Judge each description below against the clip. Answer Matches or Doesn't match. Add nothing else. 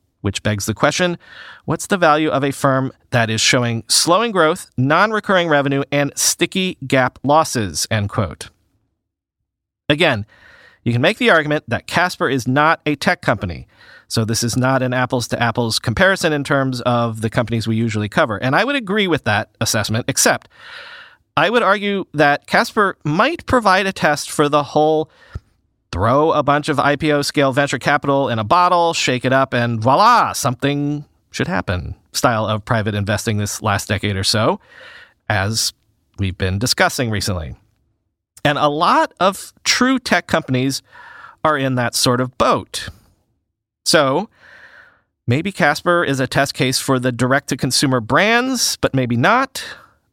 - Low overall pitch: Matches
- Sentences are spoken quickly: Doesn't match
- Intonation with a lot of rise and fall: Matches